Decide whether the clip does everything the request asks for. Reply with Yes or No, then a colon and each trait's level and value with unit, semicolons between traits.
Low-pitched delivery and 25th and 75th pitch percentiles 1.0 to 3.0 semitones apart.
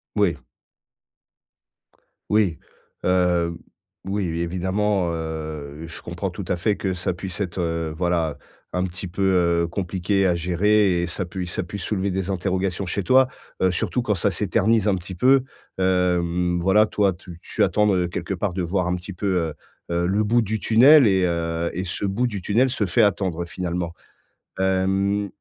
Yes: very low, 95 Hz; average, 2.7 semitones